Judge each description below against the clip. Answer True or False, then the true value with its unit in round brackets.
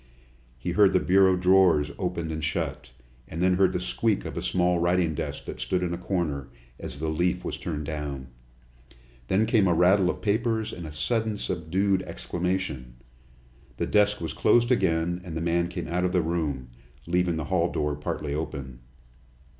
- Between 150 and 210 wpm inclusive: True (180 wpm)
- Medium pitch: False (90 Hz)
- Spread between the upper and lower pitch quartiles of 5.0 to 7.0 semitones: False (3.1 semitones)